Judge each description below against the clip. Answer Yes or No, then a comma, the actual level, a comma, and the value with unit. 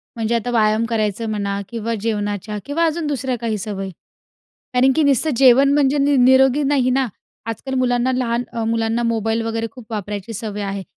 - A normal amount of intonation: Yes, average, 3.3 semitones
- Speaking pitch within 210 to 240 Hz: Yes, high, 230 Hz